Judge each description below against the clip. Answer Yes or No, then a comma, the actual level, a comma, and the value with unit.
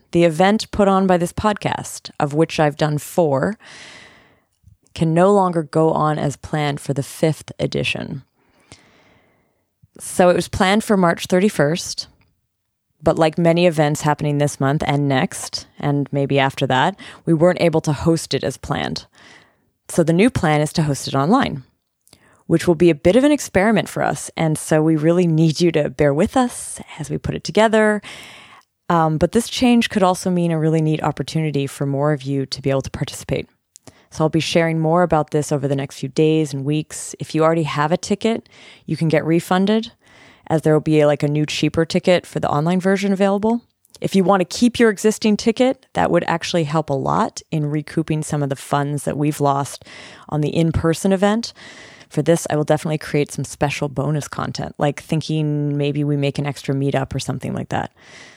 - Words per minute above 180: Yes, average, 200 wpm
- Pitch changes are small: No, average, 3.5 semitones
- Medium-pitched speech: Yes, medium, 155 Hz